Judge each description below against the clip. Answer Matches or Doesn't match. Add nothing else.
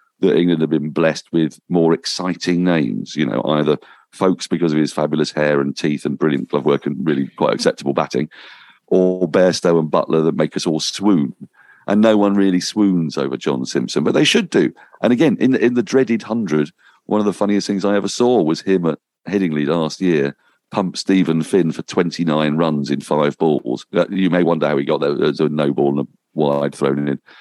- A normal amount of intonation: Matches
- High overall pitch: Doesn't match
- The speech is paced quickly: Matches